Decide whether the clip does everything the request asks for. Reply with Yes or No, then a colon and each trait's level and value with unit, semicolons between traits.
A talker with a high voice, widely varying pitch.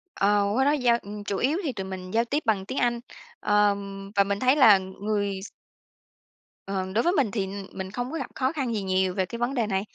No: high, 210 Hz; average, 4.4 semitones